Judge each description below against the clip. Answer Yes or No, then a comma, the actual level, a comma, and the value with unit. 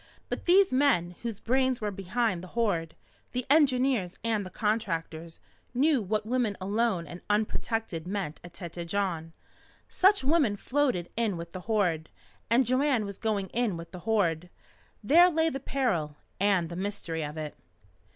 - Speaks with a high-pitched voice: Yes, high, 205 Hz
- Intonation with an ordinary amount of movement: No, wide, 6.1 semitones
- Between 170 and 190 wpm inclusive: No, average, 160 wpm